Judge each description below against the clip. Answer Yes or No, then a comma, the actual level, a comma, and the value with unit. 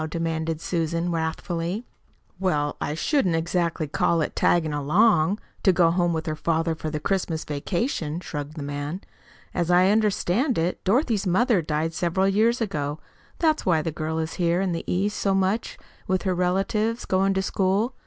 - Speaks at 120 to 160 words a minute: No, average, 170 wpm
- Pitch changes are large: No, average, 3.4 semitones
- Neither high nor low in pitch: Yes, medium, 175 Hz